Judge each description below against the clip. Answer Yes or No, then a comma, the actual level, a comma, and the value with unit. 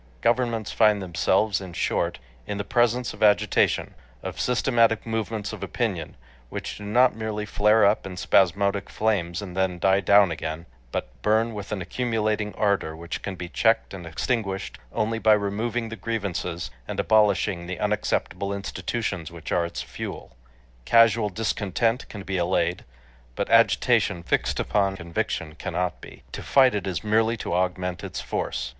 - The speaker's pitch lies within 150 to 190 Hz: No, low, 100 Hz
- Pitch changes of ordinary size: Yes, average, 3.5 semitones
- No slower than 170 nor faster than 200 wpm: No, average, 160 wpm